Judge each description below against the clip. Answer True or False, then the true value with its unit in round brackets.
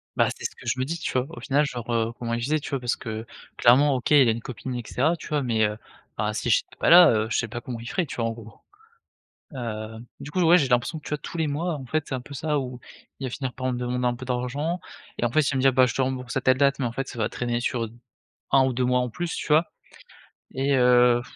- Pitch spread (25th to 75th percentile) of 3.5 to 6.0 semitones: False (2.8 semitones)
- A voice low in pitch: True (130 Hz)